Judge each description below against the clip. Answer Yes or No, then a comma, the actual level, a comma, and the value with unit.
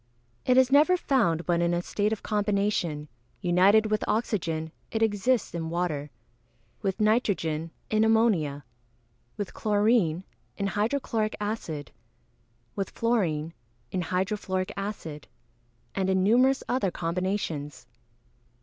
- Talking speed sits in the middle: No, slow, 125 wpm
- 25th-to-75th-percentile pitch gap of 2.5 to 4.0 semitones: No, average, 4.4 semitones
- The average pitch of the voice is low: No, high, 200 Hz